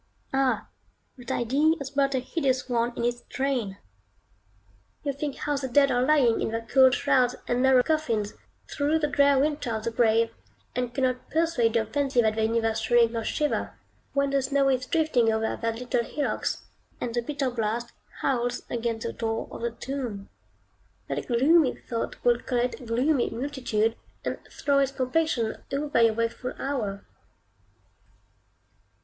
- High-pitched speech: Yes, very high, 250 Hz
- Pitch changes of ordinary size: Yes, average, 3.3 semitones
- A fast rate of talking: No, average, 165 wpm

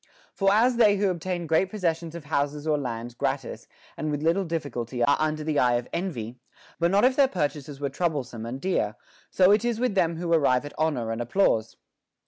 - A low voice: No, medium, 155 Hz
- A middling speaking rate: No, fast, 210 wpm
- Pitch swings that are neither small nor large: No, wide, 5.8 semitones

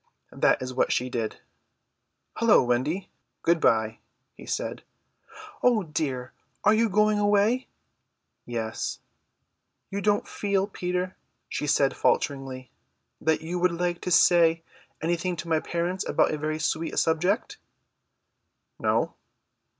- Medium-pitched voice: Yes, medium, 170 Hz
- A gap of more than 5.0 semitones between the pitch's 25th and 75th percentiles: Yes, wide, 5.4 semitones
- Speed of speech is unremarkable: No, slow, 125 wpm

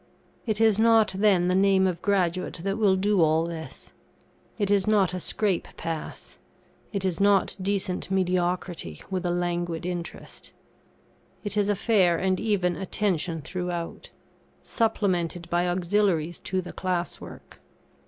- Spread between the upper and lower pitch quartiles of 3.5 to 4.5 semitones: No, narrow, 2.5 semitones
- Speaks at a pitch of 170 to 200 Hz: Yes, medium, 185 Hz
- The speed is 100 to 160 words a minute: Yes, average, 145 wpm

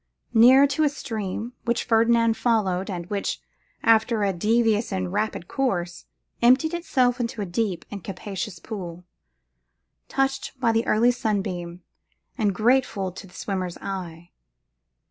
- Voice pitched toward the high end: Yes, high, 215 Hz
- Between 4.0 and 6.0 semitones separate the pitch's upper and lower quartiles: Yes, average, 4.3 semitones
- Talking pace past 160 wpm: No, slow, 135 wpm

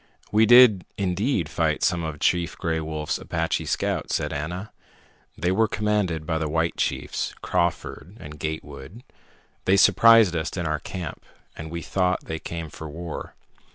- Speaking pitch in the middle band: No, very low, 85 Hz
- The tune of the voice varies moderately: Yes, average, 3.4 semitones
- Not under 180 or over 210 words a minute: No, average, 155 wpm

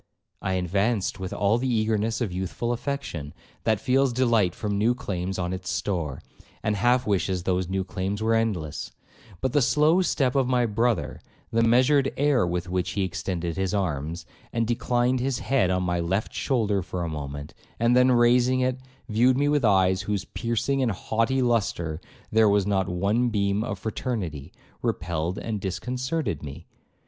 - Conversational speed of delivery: Yes, average, 175 wpm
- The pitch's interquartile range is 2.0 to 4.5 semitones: No, average, 5.1 semitones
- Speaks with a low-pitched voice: Yes, low, 105 Hz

